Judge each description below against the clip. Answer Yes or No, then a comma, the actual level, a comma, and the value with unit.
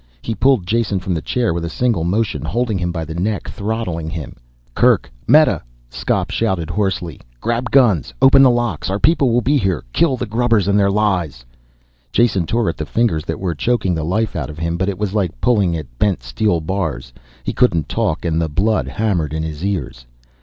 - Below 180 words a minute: No, fast, 205 wpm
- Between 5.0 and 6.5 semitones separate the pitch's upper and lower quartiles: Yes, wide, 5.6 semitones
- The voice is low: Yes, very low, 95 Hz